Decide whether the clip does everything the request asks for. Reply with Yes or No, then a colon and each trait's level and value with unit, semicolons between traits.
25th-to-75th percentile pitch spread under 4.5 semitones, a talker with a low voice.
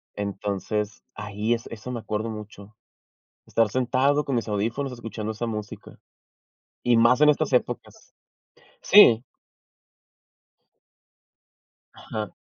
Yes: average, 2.9 semitones; low, 110 Hz